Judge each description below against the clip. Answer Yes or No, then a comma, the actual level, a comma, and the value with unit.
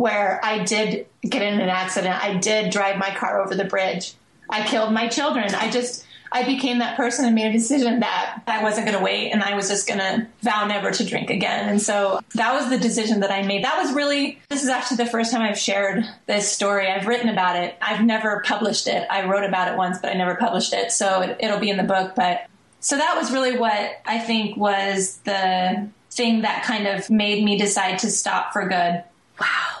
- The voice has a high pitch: Yes, high, 215 Hz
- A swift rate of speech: Yes, fast, 230 wpm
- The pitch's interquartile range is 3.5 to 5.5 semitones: No, average, 3.1 semitones